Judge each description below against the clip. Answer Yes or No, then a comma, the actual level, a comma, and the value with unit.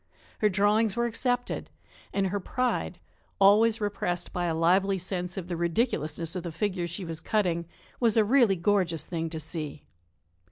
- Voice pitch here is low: No, high, 190 Hz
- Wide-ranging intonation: No, average, 3.8 semitones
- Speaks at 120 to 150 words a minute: No, average, 165 wpm